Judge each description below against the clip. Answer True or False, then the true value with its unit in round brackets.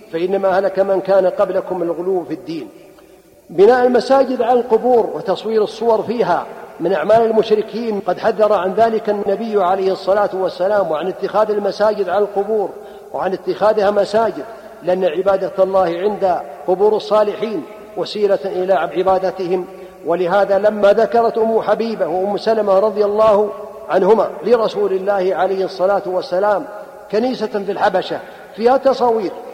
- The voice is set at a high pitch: True (205 Hz)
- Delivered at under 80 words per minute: False (130 wpm)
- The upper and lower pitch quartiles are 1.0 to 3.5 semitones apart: True (2.5 semitones)